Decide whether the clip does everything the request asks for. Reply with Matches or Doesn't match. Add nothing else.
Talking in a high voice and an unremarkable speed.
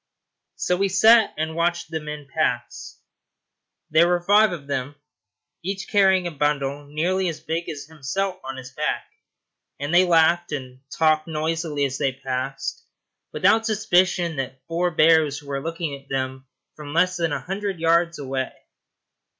Doesn't match